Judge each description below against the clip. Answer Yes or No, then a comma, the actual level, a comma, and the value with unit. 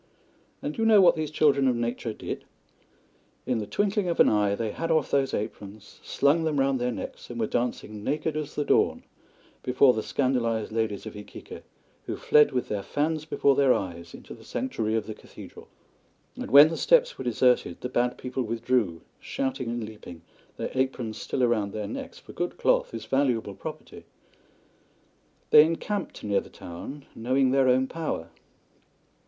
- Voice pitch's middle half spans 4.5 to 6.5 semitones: Yes, average, 5.0 semitones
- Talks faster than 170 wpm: Yes, average, 180 wpm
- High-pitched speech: No, low, 125 Hz